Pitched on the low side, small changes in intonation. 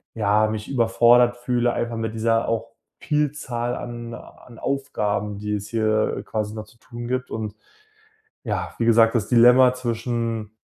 Yes: low, 115 Hz; narrow, 2.0 semitones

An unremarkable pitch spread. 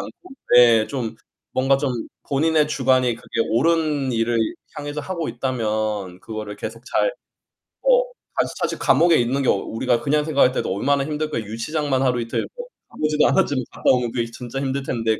Yes: average, 4.4 semitones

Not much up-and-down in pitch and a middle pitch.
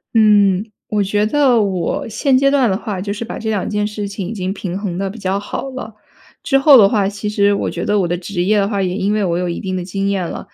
No: narrow, 2.1 semitones; high, 205 Hz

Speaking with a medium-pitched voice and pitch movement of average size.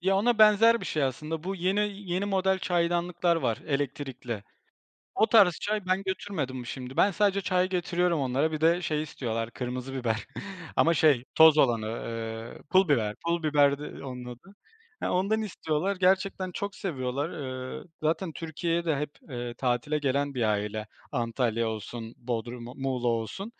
No: medium, 150 Hz; wide, 7.0 semitones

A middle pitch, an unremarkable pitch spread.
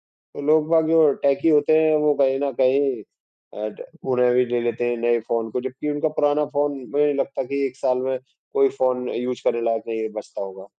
No: low, 130 Hz; average, 3.3 semitones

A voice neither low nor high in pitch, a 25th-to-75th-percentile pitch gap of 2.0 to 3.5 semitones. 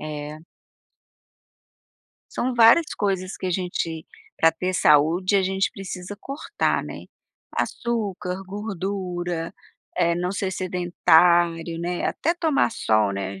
Yes: medium, 180 Hz; average, 2.9 semitones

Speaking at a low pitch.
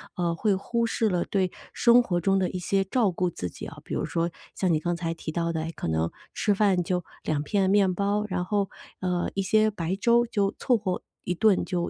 No: medium, 185 Hz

